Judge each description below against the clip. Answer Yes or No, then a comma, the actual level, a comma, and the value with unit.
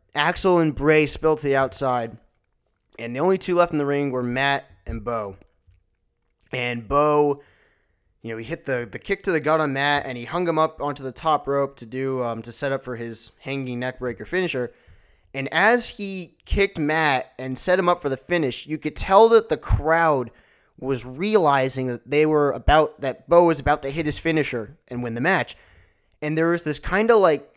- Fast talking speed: Yes, fast, 210 wpm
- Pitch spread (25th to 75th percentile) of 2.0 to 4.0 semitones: No, average, 4.5 semitones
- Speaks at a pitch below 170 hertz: Yes, medium, 140 Hz